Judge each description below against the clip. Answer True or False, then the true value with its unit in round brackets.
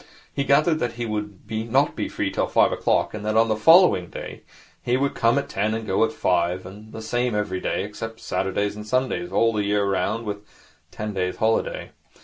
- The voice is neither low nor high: False (110 Hz)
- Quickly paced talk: True (215 wpm)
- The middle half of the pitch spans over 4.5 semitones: False (2.8 semitones)